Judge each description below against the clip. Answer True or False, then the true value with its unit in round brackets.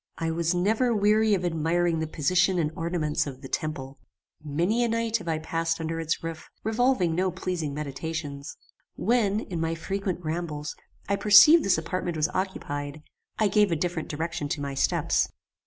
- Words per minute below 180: True (170 wpm)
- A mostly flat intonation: False (3.9 semitones)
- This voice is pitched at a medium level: True (170 Hz)